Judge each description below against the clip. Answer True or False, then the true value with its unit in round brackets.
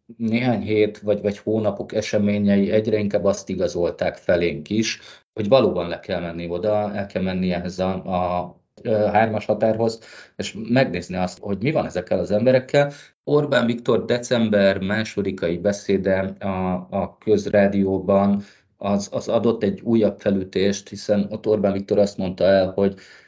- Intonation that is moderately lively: False (2.0 semitones)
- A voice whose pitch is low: True (100 Hz)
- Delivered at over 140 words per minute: True (150 wpm)